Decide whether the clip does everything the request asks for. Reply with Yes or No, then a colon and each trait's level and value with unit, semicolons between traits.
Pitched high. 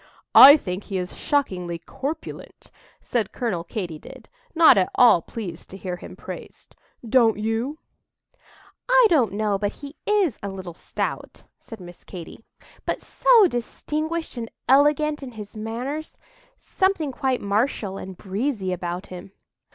Yes: high, 225 Hz